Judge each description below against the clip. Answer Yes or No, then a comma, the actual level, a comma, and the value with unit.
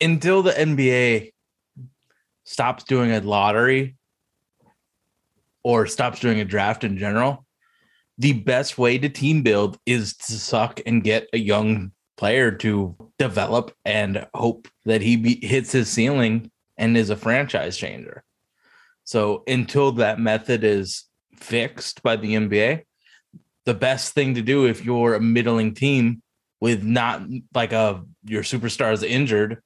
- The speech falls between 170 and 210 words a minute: No, average, 140 wpm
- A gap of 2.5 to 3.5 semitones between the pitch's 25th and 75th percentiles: Yes, average, 3.1 semitones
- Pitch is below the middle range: Yes, low, 115 Hz